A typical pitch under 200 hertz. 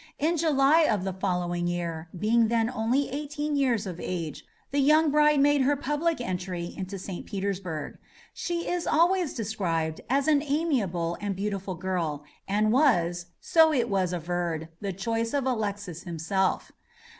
No: high, 210 Hz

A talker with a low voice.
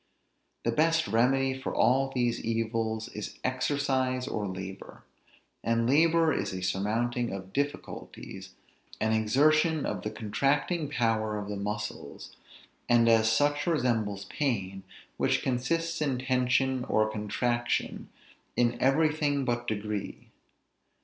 Yes: low, 120 Hz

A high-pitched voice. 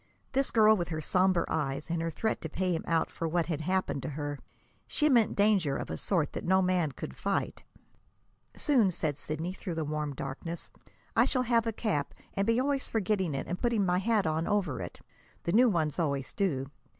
No: medium, 175 Hz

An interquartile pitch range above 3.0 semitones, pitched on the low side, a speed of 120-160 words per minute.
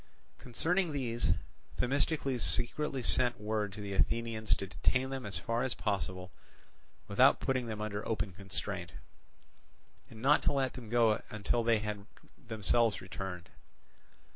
Yes: average, 3.7 semitones; low, 115 Hz; average, 140 wpm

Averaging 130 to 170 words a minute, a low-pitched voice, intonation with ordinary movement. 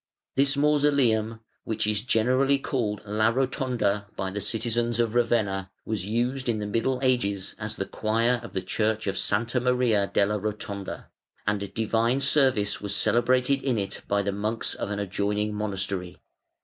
Yes: average, 160 wpm; low, 110 Hz; average, 3.4 semitones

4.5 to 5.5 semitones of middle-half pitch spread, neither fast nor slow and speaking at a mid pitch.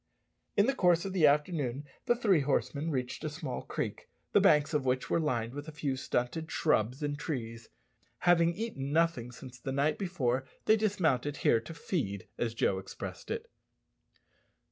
Yes: average, 4.9 semitones; average, 170 wpm; medium, 145 Hz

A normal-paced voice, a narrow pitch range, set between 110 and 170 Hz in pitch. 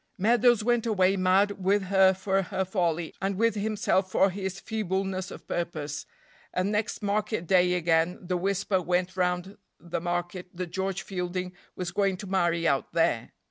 No: average, 165 wpm; narrow, 1.9 semitones; high, 190 Hz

